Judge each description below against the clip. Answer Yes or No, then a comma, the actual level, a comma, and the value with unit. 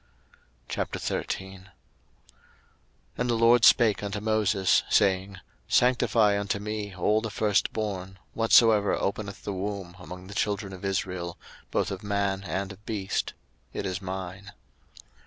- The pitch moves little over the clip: Yes, narrow, 1.9 semitones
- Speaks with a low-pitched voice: Yes, low, 100 Hz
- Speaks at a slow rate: Yes, slow, 130 wpm